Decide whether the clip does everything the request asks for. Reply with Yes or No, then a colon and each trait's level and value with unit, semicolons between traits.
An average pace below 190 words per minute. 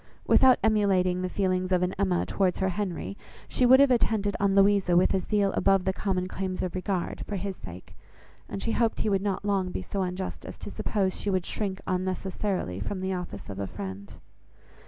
No: fast, 205 wpm